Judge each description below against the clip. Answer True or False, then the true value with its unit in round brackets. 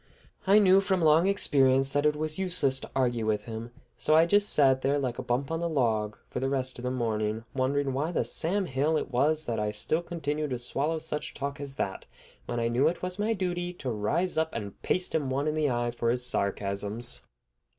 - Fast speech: True (225 wpm)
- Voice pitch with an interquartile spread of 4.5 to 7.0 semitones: True (4.9 semitones)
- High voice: False (140 Hz)